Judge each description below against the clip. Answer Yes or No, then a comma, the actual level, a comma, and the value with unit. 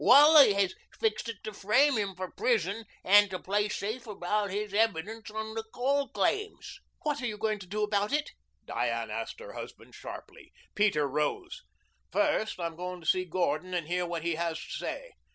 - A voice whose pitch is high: Yes, high, 210 Hz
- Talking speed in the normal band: Yes, average, 190 wpm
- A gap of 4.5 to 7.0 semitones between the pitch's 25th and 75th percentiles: Yes, average, 4.8 semitones